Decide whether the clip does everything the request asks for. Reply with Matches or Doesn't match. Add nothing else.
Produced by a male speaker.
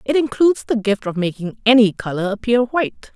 Doesn't match